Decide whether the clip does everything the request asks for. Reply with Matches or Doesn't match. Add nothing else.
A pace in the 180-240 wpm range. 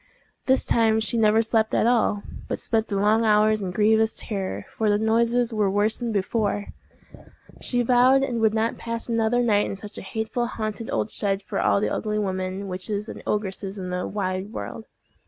Matches